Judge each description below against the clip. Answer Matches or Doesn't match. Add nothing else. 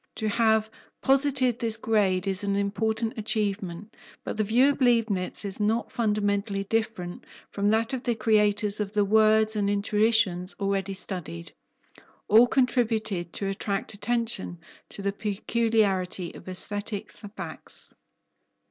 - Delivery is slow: Matches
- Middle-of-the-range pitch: Doesn't match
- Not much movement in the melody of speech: Matches